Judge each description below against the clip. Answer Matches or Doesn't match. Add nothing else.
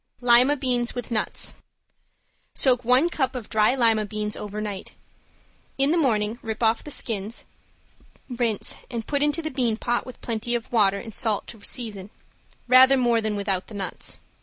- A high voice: Matches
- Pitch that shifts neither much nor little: Matches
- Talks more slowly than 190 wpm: Matches